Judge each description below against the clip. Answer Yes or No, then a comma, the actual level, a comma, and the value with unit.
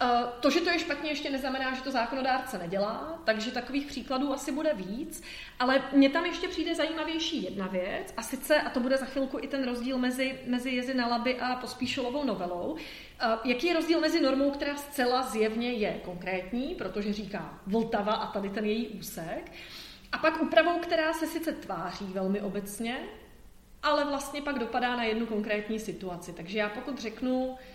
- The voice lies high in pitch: Yes, very high, 255 Hz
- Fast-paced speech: Yes, fast, 175 wpm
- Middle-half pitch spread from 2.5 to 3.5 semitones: No, average, 4.9 semitones